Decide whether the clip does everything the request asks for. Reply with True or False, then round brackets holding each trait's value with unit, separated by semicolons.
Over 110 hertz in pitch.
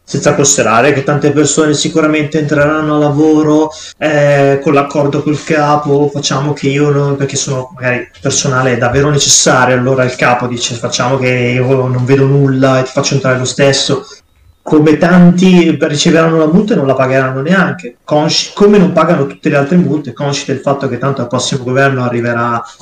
True (140 Hz)